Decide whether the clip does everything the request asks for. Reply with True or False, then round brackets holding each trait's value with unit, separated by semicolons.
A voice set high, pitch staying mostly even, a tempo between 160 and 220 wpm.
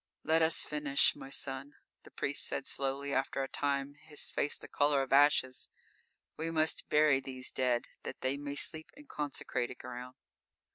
False (140 Hz; 2.0 semitones; 165 wpm)